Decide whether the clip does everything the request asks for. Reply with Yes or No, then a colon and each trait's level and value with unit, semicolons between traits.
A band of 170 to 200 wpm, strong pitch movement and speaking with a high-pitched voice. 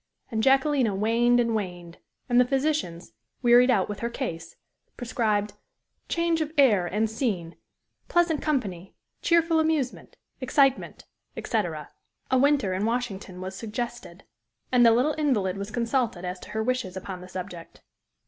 No: average, 145 wpm; wide, 5.7 semitones; high, 235 Hz